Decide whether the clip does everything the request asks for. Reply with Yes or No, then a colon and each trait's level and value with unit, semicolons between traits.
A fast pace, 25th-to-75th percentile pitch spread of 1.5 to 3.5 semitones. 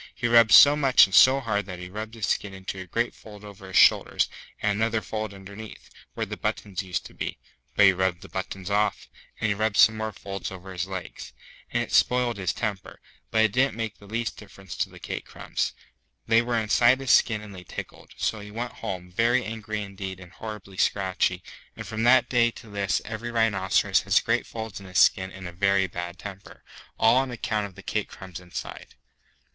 Yes: fast, 215 wpm; average, 2.9 semitones